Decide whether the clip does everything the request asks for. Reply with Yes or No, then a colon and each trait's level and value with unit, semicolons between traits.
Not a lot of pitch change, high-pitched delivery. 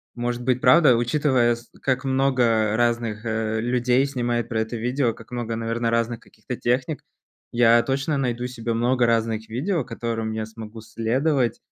No: narrow, 1.8 semitones; low, 120 Hz